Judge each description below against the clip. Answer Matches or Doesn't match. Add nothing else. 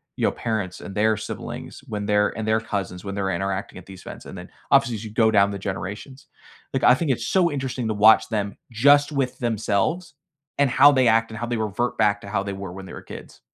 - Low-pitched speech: Matches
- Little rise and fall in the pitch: Doesn't match